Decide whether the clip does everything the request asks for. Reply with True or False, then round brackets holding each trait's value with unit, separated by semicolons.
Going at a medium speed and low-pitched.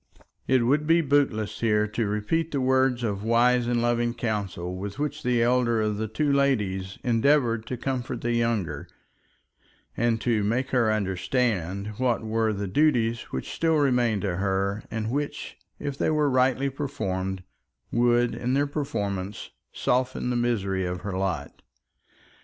True (155 wpm; 115 Hz)